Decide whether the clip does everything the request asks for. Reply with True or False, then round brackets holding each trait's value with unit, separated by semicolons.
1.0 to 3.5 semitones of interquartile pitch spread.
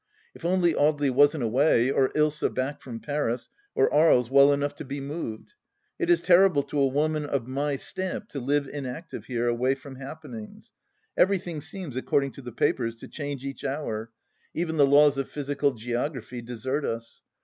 True (3.0 semitones)